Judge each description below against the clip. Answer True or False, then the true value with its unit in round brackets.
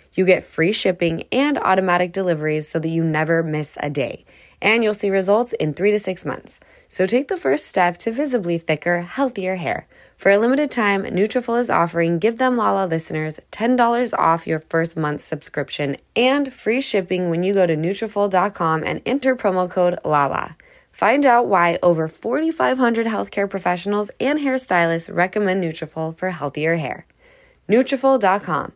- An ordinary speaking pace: True (165 wpm)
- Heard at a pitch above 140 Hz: True (190 Hz)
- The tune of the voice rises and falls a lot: True (5.9 semitones)